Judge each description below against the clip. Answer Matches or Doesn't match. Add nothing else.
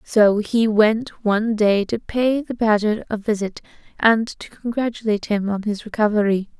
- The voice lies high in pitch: Matches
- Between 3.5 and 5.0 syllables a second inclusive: Matches